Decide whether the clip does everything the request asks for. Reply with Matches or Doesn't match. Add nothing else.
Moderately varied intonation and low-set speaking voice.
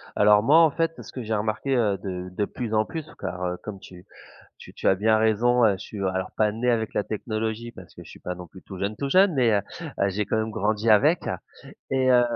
Matches